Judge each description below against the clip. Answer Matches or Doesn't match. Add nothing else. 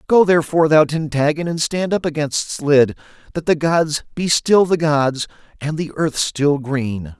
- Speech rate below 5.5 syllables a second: Matches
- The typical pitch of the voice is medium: Matches